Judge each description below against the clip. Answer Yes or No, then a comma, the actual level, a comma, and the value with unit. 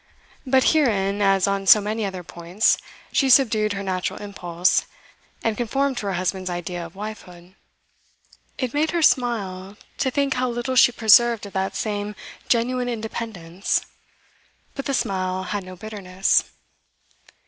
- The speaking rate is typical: Yes, average, 145 wpm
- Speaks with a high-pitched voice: Yes, high, 205 Hz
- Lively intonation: No, average, 4.3 semitones